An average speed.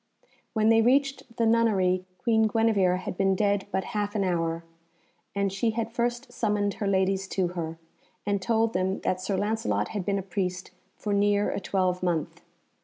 Yes: average, 175 wpm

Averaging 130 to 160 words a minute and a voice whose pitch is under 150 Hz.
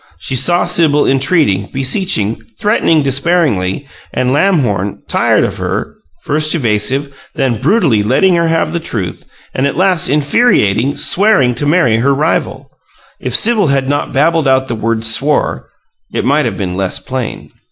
Yes: average, 150 wpm; medium, 140 Hz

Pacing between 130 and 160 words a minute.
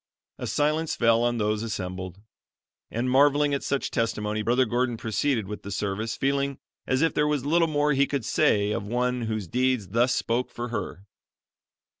No: average, 180 wpm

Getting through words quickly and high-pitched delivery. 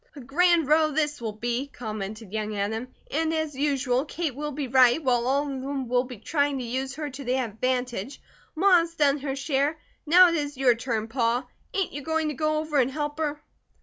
Yes: fast, 215 wpm; very high, 275 Hz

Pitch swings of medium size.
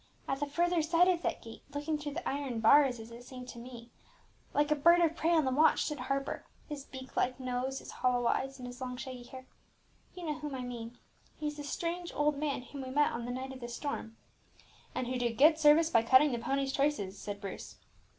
Yes: average, 3.3 semitones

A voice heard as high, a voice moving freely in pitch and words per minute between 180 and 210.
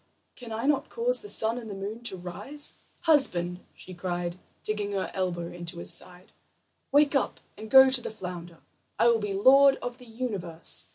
Yes: high, 215 Hz; wide, 6.5 semitones; average, 185 wpm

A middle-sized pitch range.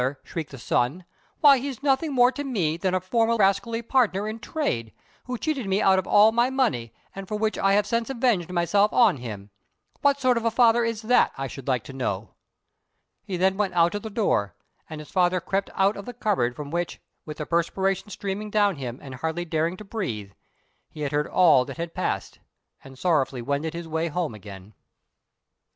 No: wide, 6.9 semitones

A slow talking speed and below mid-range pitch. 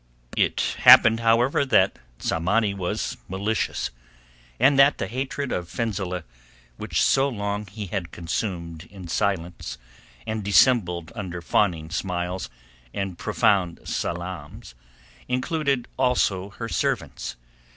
Yes: slow, 110 wpm; low, 100 Hz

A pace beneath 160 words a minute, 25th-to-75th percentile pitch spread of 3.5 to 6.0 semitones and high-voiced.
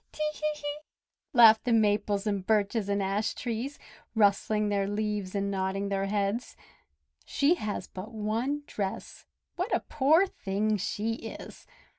No: average, 140 wpm; average, 2.8 semitones; high, 210 Hz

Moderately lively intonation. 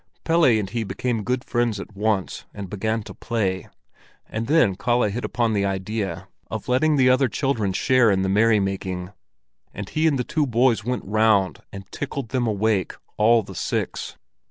Yes: average, 4.2 semitones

